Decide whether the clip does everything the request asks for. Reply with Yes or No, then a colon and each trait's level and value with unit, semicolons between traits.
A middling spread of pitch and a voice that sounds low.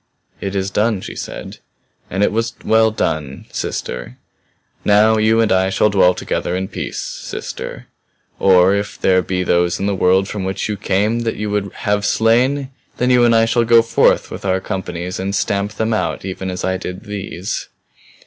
Yes: average, 3.0 semitones; low, 100 Hz